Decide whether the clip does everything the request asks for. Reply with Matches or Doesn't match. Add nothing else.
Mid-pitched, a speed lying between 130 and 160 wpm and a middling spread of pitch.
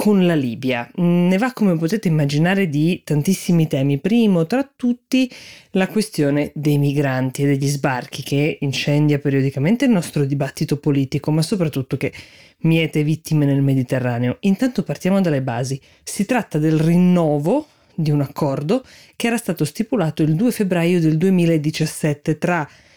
Matches